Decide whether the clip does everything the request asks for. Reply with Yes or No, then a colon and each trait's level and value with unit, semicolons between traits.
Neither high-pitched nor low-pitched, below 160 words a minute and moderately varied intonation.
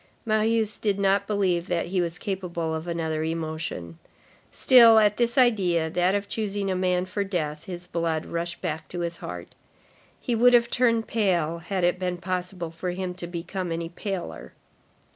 No: medium, 180 Hz; average, 175 wpm; average, 3.2 semitones